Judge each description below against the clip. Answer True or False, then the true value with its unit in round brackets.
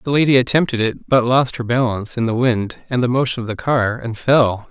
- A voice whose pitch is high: False (120 Hz)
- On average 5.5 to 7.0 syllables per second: True (5.6 syllables/s)